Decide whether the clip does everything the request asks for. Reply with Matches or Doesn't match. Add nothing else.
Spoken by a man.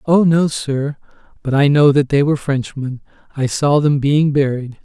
Matches